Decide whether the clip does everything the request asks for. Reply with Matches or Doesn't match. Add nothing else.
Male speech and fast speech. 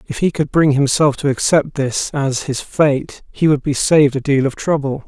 Matches